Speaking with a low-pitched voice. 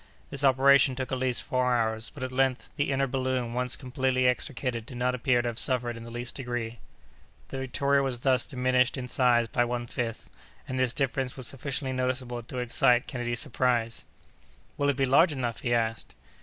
Yes: low, 125 Hz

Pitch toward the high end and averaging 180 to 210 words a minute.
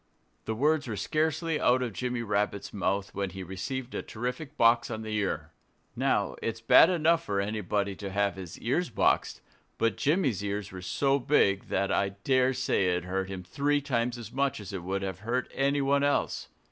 No: low, 115 Hz; average, 190 wpm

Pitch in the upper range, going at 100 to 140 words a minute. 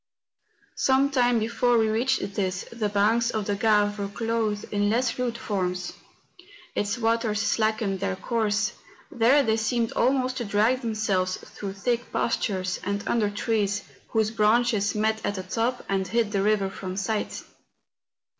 No: high, 215 Hz; average, 155 wpm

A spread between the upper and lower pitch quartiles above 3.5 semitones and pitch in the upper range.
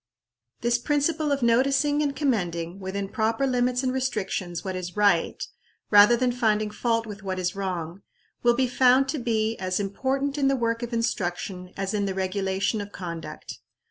Yes: average, 5.0 semitones; high, 220 Hz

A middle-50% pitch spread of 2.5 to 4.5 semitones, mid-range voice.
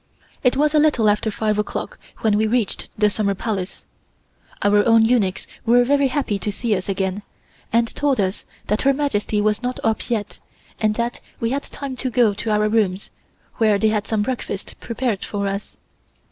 No: average, 3.0 semitones; high, 220 Hz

